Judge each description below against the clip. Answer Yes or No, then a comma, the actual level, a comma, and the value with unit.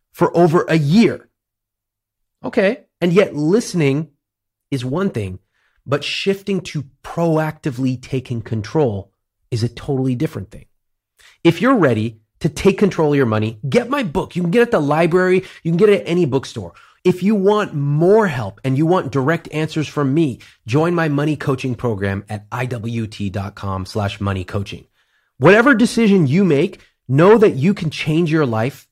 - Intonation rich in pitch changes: Yes, wide, 7.6 semitones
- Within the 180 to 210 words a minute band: No, average, 165 wpm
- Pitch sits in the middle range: Yes, medium, 145 Hz